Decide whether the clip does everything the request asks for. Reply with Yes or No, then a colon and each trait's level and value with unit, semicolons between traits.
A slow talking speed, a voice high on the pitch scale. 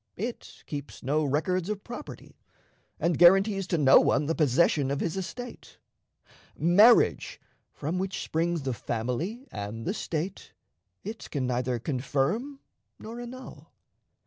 No: slow, 130 wpm; medium, 170 Hz